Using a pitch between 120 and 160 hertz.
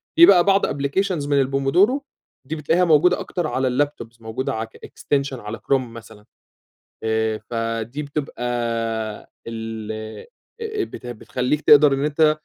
Yes: low, 135 Hz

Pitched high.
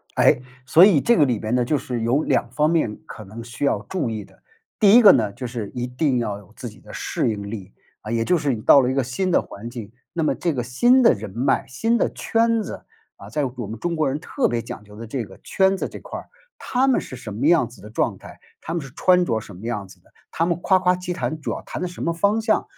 No: low, 130 Hz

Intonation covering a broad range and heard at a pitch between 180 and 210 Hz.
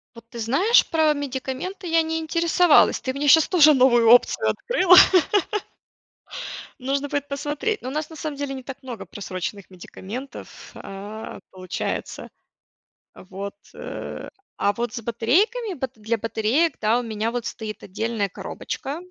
No: wide, 5.7 semitones; very high, 260 Hz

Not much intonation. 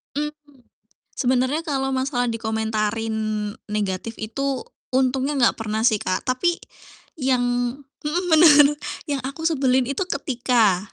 No: average, 3.9 semitones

